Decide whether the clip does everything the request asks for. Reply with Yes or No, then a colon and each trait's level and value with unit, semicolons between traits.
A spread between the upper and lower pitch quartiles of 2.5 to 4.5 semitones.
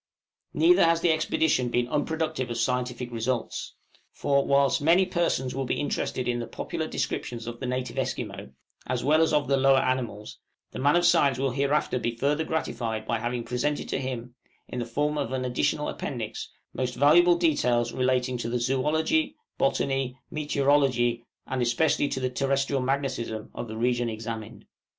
Yes: average, 3.2 semitones